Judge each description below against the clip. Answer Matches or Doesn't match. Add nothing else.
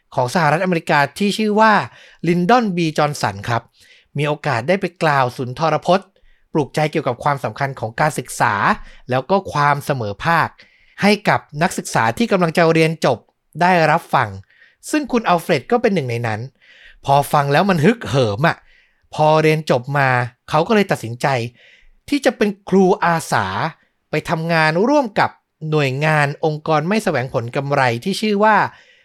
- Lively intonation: Doesn't match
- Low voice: Doesn't match